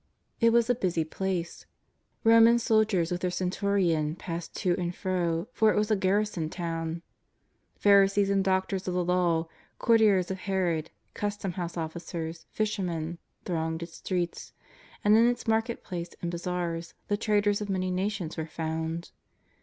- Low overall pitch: No, medium, 185 Hz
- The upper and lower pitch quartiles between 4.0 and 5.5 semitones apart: No, average, 3.4 semitones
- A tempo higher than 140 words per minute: Yes, average, 160 wpm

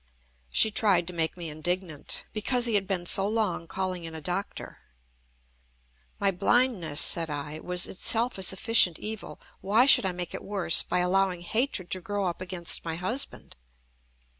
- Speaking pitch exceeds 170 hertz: Yes, medium, 185 Hz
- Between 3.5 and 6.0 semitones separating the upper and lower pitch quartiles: No, average, 3.1 semitones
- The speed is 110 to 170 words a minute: Yes, average, 165 wpm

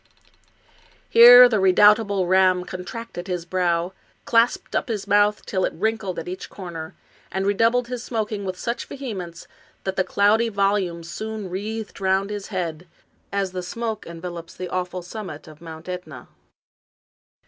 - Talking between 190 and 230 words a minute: No, average, 150 wpm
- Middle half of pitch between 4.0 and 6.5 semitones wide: No, average, 3.3 semitones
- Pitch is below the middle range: No, high, 190 Hz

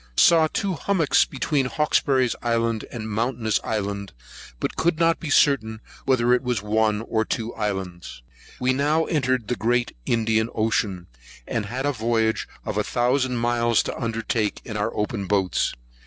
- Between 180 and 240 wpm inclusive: No, average, 155 wpm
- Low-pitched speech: Yes, low, 115 Hz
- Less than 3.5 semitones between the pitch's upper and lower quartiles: Yes, average, 3.1 semitones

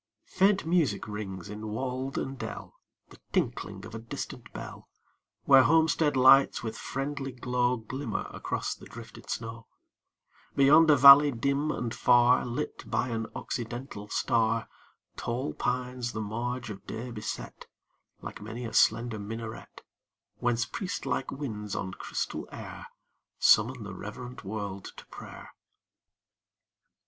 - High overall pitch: No, low, 120 Hz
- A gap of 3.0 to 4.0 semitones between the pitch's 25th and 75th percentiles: Yes, average, 3.5 semitones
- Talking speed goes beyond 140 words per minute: No, slow, 135 wpm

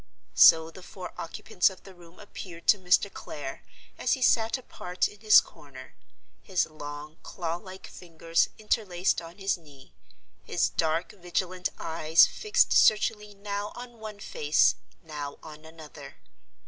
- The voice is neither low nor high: Yes, medium, 180 Hz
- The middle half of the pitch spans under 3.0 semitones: No, average, 4.0 semitones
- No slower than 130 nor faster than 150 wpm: Yes, average, 145 wpm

